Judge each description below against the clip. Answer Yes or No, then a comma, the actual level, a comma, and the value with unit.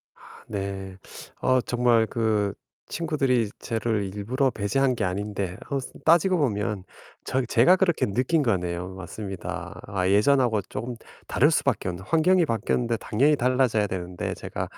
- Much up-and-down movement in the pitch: No, average, 5.0 semitones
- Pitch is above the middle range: No, low, 115 Hz